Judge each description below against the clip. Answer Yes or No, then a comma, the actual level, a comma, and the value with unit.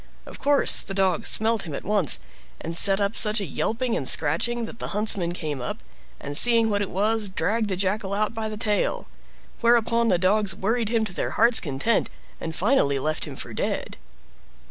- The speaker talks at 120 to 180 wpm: No, average, 195 wpm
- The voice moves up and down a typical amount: Yes, average, 3.9 semitones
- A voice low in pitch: No, high, 205 Hz